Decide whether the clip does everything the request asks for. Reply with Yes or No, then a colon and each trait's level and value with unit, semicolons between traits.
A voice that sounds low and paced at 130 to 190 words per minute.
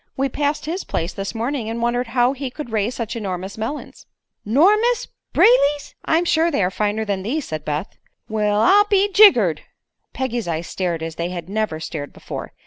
No: high, 230 Hz; average, 185 wpm